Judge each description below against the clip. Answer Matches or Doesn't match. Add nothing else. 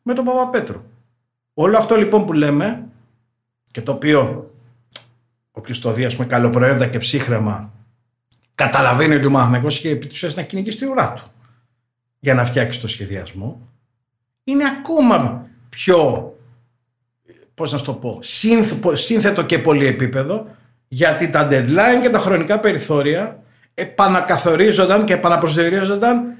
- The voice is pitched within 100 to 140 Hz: Matches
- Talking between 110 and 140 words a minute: Matches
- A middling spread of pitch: Doesn't match